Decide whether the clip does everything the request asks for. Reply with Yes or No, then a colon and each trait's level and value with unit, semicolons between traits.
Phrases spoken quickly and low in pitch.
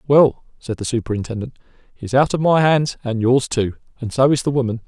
Yes: fast, 220 wpm; low, 125 Hz